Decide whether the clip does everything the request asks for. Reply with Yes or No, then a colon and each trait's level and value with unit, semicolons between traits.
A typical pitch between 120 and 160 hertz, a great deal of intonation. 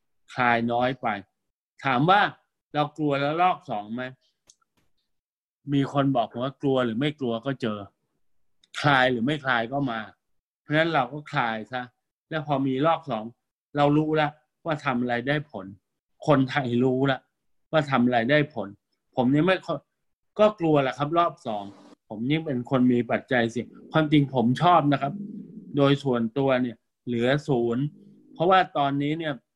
No: medium, 140 Hz; average, 3.7 semitones